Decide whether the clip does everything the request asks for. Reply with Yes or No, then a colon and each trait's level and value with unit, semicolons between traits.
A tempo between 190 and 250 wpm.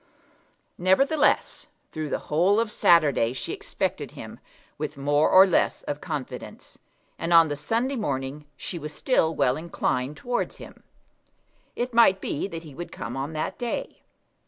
No: average, 155 wpm